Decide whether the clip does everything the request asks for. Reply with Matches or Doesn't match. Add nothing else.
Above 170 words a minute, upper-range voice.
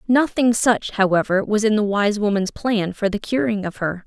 Matches